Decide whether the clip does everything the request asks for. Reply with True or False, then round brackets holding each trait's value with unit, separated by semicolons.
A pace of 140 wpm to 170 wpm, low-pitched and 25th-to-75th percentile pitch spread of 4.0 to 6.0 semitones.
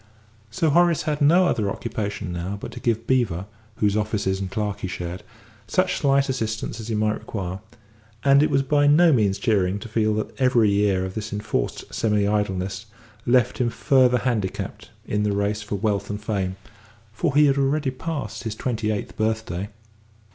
False (180 wpm; 110 Hz; 4.3 semitones)